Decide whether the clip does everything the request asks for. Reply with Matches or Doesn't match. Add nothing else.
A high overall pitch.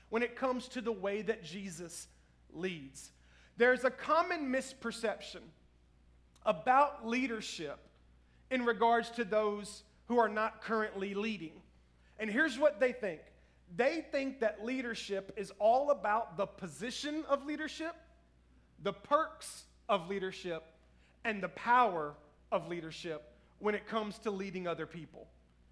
Matches